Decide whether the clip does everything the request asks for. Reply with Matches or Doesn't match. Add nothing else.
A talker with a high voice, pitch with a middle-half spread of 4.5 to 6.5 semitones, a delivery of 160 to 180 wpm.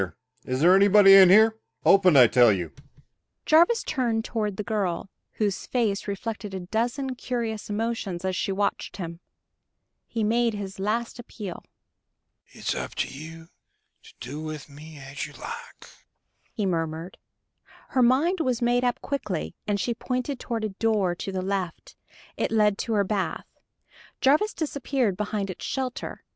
Doesn't match